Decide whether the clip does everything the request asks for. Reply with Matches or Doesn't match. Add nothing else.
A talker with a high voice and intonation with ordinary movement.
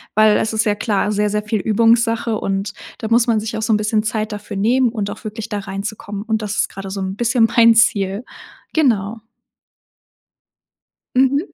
Doesn't match